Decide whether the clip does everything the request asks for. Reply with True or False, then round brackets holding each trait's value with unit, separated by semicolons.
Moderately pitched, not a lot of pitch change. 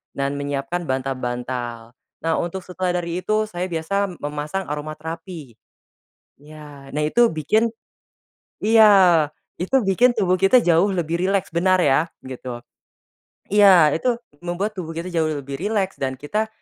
False (170 Hz; 4.7 semitones)